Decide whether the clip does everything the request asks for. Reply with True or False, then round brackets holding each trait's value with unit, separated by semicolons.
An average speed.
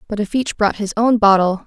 False (255 wpm)